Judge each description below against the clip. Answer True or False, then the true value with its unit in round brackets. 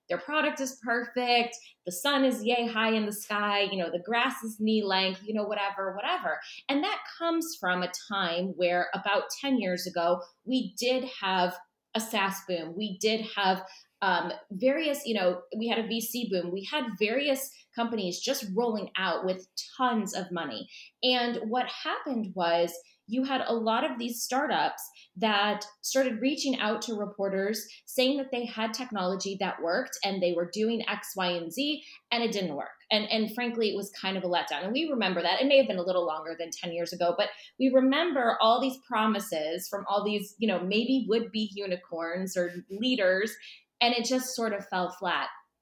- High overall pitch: True (215 Hz)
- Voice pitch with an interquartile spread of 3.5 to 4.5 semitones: False (5.0 semitones)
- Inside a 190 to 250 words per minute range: True (195 wpm)